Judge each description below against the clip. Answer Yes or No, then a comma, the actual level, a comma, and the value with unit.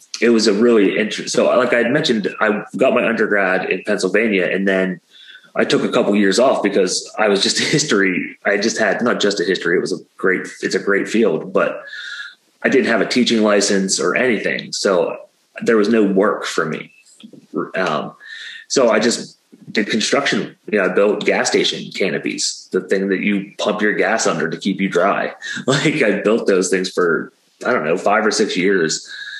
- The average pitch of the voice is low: Yes, low, 105 Hz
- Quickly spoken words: Yes, fast, 200 wpm